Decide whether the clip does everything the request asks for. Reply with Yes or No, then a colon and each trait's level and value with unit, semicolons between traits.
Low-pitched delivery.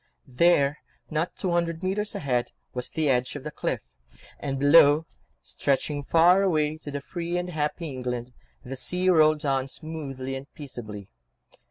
No: medium, 150 Hz